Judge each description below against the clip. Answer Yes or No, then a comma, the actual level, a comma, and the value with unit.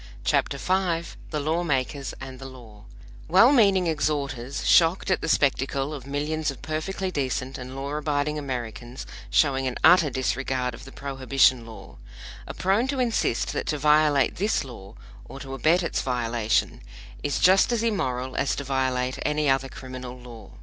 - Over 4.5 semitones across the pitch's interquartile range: No, average, 3.5 semitones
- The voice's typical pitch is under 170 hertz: Yes, medium, 140 Hz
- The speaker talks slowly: No, average, 165 wpm